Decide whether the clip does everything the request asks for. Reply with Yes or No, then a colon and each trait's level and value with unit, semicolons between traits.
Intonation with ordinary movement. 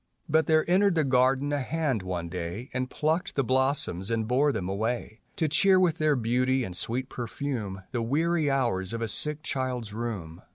Yes: average, 5.0 semitones